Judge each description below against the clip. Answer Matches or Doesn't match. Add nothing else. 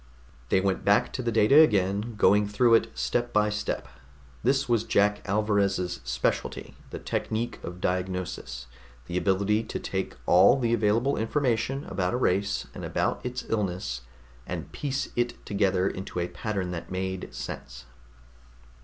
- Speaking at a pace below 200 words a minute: Matches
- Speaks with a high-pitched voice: Doesn't match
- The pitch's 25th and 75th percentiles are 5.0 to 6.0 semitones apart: Doesn't match